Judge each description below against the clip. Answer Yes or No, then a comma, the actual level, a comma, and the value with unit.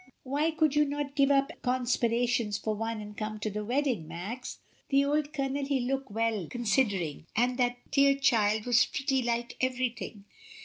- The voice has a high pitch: Yes, high, 245 Hz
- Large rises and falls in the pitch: No, average, 4.1 semitones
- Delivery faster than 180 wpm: No, average, 170 wpm